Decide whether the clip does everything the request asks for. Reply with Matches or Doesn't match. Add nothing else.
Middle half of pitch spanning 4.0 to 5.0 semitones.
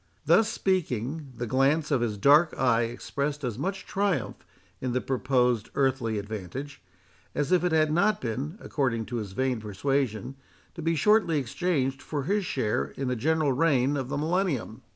Matches